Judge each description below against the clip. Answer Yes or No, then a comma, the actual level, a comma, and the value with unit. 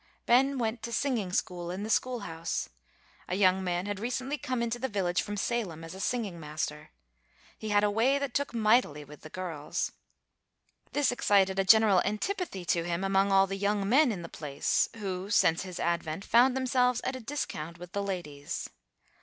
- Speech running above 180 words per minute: Yes, average, 190 wpm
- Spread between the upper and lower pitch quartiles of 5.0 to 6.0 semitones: Yes, average, 5.3 semitones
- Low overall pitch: No, high, 200 Hz